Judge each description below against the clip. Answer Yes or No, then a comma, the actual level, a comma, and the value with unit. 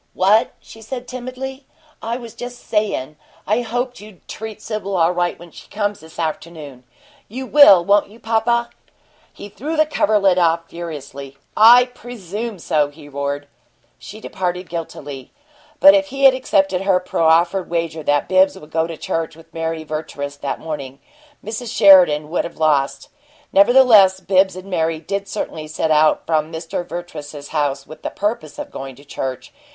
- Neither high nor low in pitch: Yes, medium, 180 Hz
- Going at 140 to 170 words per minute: Yes, average, 165 wpm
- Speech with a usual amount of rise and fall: No, wide, 5.8 semitones